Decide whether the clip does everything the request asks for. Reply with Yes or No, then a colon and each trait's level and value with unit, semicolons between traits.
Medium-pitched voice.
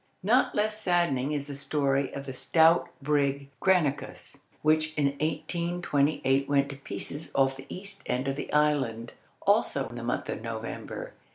Yes: medium, 145 Hz